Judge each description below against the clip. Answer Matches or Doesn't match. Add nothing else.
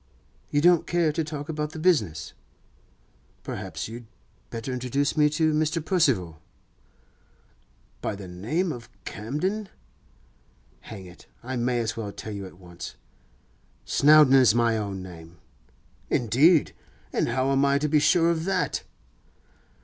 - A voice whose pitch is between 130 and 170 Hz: Matches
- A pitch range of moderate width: Doesn't match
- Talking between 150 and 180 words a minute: Doesn't match